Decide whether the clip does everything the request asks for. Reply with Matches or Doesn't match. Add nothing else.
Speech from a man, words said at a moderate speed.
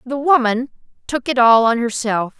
Doesn't match